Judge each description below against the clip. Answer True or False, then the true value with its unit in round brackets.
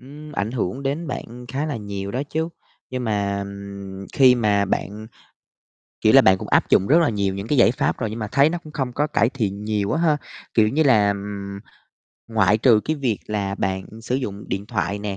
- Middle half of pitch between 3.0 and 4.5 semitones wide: False (5.1 semitones)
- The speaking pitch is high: False (110 Hz)